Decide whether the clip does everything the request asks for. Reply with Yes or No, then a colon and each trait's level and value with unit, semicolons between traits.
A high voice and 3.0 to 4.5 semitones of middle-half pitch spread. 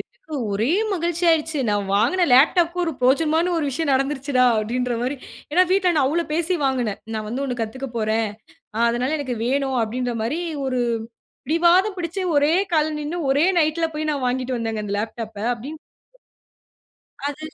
No: very high, 280 Hz; average, 4.9 semitones